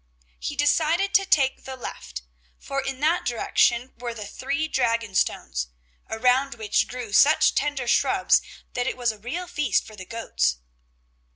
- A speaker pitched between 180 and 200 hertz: No, very high, 250 Hz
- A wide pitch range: No, average, 4.5 semitones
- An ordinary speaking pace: Yes, average, 160 wpm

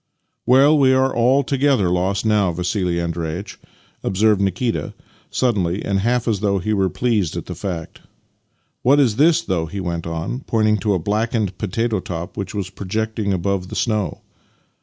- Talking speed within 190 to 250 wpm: No, average, 175 wpm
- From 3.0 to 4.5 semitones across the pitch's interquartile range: Yes, average, 4.2 semitones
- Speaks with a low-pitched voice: Yes, low, 100 Hz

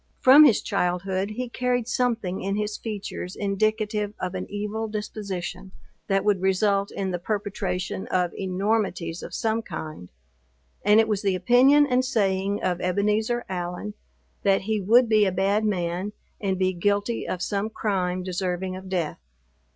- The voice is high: Yes, high, 200 Hz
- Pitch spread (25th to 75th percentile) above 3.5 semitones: No, average, 2.7 semitones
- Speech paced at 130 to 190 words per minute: Yes, average, 155 wpm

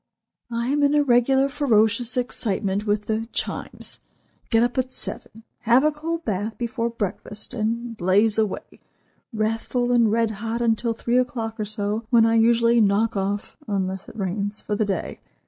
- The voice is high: Yes, high, 225 Hz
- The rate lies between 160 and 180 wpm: Yes, average, 165 wpm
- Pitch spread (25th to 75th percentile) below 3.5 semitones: Yes, narrow, 2.4 semitones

